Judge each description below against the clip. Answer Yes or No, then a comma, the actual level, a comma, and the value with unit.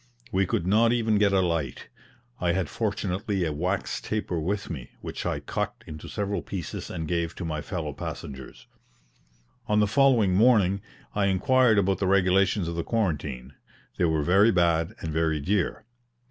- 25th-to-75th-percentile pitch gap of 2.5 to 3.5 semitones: No, average, 3.9 semitones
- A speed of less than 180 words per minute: Yes, average, 170 wpm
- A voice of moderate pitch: No, very low, 95 Hz